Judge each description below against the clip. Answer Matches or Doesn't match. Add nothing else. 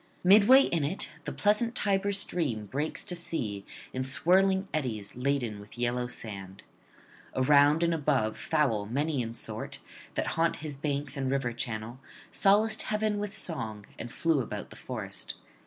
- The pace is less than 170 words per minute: Matches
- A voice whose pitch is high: Doesn't match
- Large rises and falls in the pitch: Matches